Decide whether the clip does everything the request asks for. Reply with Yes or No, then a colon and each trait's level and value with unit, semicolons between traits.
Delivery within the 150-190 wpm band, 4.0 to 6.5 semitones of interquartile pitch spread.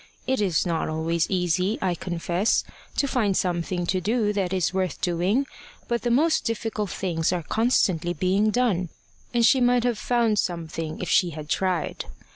Yes: average, 170 wpm; average, 4.8 semitones